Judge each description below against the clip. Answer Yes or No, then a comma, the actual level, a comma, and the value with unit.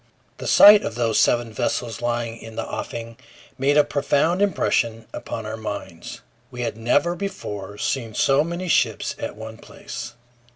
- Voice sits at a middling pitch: No, low, 120 Hz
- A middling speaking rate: Yes, average, 160 wpm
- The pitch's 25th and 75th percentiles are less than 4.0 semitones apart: No, average, 4.5 semitones